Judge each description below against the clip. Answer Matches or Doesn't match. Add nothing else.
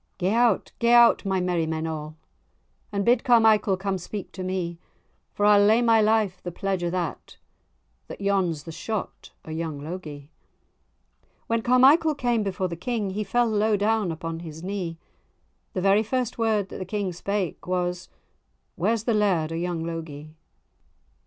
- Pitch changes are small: Doesn't match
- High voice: Matches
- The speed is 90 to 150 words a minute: Doesn't match